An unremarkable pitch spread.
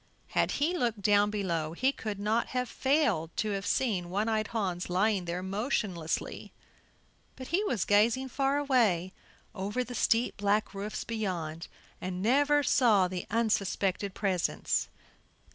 Yes: average, 4.3 semitones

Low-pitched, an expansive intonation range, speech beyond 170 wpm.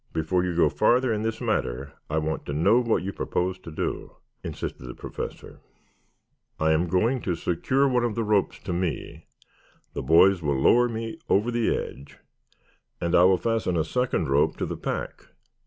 Yes: very low, 90 Hz; wide, 6.2 semitones; average, 185 wpm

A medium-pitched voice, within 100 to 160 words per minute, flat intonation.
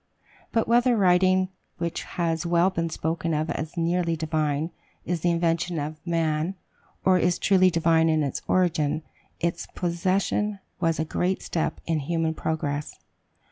Yes: medium, 170 Hz; average, 145 wpm; narrow, 2.1 semitones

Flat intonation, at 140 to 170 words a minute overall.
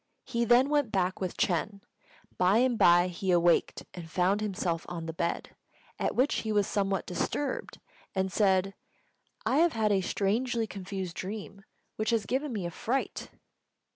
No: average, 4.1 semitones; average, 165 wpm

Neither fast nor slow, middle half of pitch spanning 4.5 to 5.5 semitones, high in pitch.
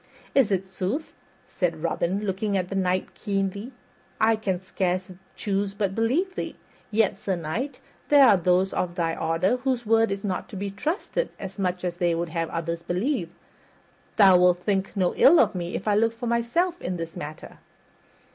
No: average, 175 wpm; average, 4.0 semitones; high, 195 Hz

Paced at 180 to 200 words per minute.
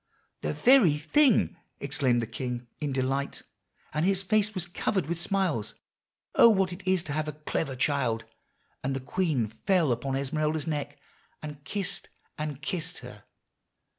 No: average, 155 wpm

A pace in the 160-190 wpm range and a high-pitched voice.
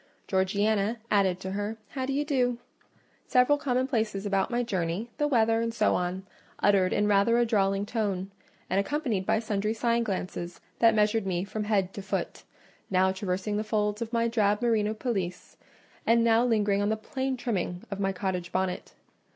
Yes: average, 170 wpm; high, 210 Hz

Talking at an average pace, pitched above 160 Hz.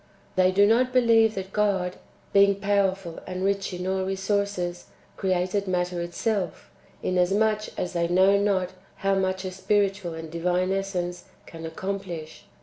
Yes: average, 145 wpm; high, 190 Hz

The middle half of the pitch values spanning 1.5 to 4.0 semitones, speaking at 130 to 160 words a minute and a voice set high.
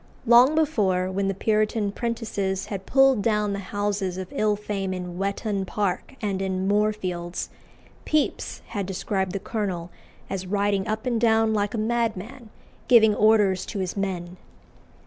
Yes: narrow, 2.5 semitones; average, 150 wpm; high, 205 Hz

